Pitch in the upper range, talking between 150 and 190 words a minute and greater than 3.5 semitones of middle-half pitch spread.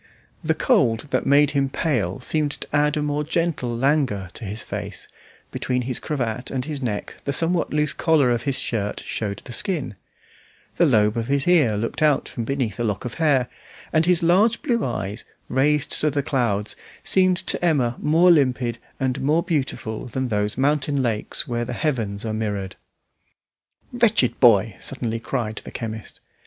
No: low, 130 Hz; average, 175 wpm; average, 4.9 semitones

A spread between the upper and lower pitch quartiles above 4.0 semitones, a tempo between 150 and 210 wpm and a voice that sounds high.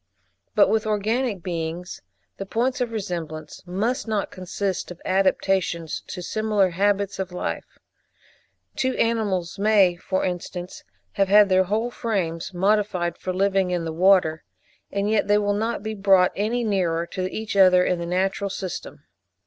No: average, 2.8 semitones; average, 155 wpm; high, 195 Hz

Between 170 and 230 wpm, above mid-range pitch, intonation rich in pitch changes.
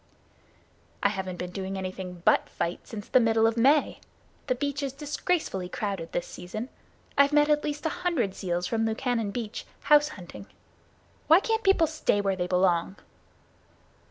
No: average, 160 wpm; high, 225 Hz; wide, 7.7 semitones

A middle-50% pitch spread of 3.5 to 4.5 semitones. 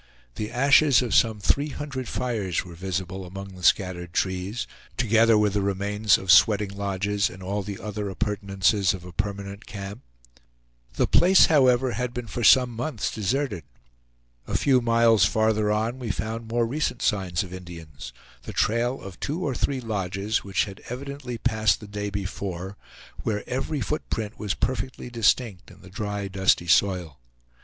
Yes: average, 3.9 semitones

